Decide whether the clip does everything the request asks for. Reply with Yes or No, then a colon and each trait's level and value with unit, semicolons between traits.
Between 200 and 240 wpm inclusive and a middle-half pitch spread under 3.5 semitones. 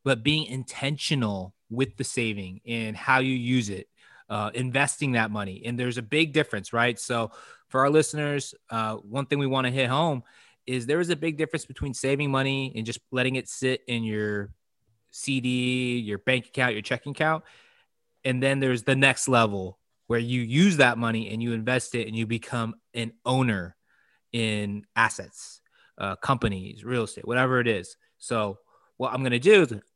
No: average, 185 wpm; average, 3.0 semitones